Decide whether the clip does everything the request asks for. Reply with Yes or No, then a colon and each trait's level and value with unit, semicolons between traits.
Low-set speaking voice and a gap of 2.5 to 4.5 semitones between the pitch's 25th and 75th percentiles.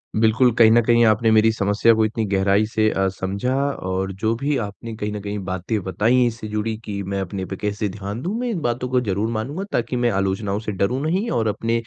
Yes: low, 110 Hz; average, 2.9 semitones